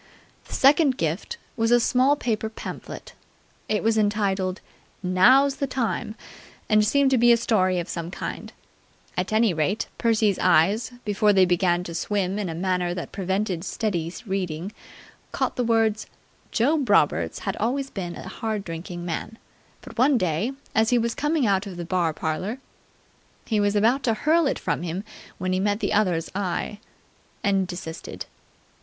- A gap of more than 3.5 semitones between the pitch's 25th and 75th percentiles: Yes, average, 4.2 semitones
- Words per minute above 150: Yes, average, 170 wpm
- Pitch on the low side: No, high, 205 Hz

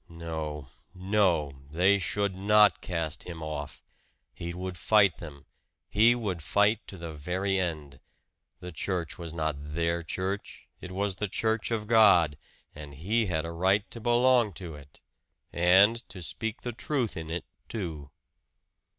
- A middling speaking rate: Yes, average, 150 wpm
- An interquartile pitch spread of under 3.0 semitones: No, average, 4.3 semitones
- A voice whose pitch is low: Yes, very low, 90 Hz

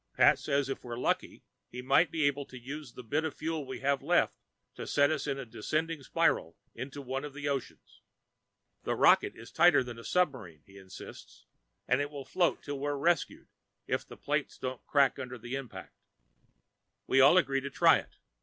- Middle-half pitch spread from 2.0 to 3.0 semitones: Yes, narrow, 2.6 semitones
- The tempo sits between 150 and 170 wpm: No, average, 195 wpm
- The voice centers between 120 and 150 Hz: Yes, medium, 140 Hz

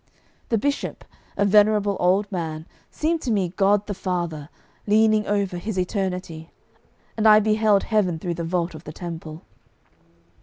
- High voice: Yes, high, 195 Hz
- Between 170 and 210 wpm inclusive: No, average, 150 wpm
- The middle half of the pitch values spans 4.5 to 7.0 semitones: No, average, 3.6 semitones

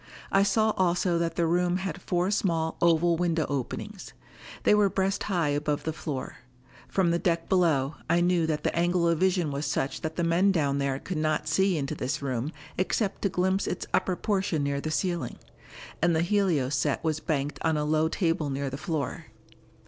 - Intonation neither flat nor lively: Yes, average, 3.4 semitones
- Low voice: No, medium, 165 Hz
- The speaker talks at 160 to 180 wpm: No, average, 195 wpm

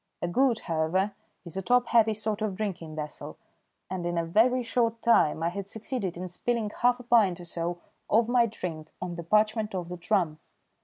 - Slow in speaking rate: No, average, 200 wpm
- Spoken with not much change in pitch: No, average, 4.9 semitones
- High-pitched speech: Yes, high, 200 Hz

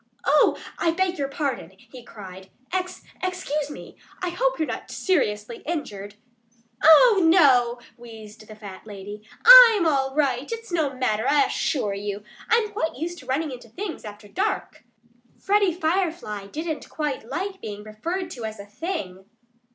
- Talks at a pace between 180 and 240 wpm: No, average, 155 wpm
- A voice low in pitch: No, very high, 280 Hz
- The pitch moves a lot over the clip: Yes, wide, 8.6 semitones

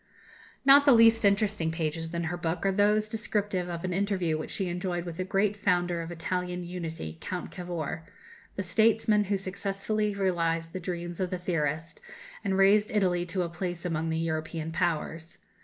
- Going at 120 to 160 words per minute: No, average, 175 wpm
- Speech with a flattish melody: No, average, 3.1 semitones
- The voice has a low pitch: No, medium, 180 Hz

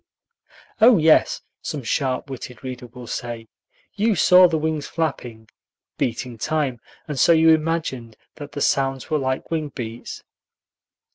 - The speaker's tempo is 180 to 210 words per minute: No, average, 140 wpm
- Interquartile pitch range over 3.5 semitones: Yes, average, 4.4 semitones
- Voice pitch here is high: No, medium, 140 Hz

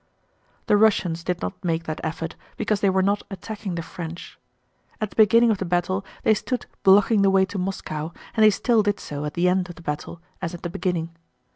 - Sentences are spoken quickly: Yes, fast, 220 wpm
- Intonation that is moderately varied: Yes, average, 3.5 semitones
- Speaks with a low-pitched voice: No, medium, 185 Hz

